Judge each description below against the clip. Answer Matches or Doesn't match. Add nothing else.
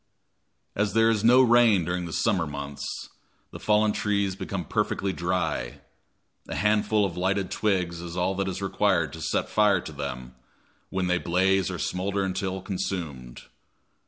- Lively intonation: Doesn't match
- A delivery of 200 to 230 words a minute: Doesn't match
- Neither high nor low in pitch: Doesn't match